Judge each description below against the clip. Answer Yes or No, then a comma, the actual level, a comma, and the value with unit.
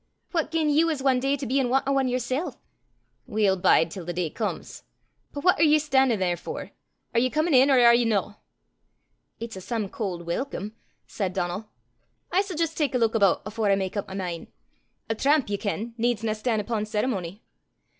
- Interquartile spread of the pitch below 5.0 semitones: No, average, 5.3 semitones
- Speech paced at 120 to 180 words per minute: No, fast, 205 wpm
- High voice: Yes, high, 230 Hz